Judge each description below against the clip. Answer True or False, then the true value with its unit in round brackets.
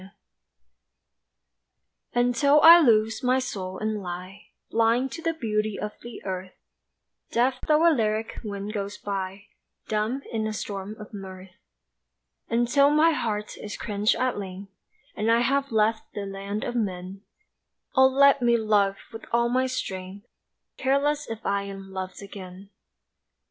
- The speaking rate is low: False (150 wpm)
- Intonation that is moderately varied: True (4.2 semitones)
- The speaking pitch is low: False (215 Hz)